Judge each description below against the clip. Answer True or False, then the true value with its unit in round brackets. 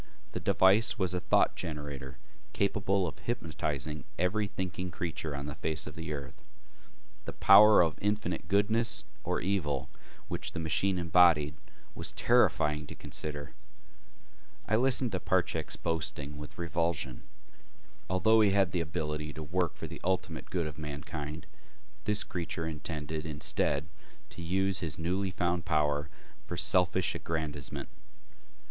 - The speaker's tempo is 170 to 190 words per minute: False (140 wpm)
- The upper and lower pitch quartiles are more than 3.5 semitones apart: True (3.9 semitones)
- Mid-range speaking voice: False (85 Hz)